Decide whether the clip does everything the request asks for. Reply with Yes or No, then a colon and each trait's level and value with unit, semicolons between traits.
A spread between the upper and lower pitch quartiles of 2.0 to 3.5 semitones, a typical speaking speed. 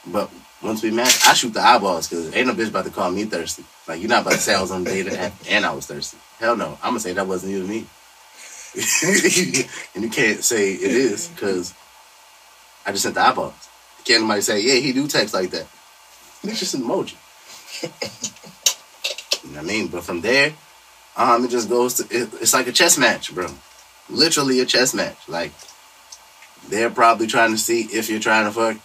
No: narrow, 2.4 semitones; fast, 210 wpm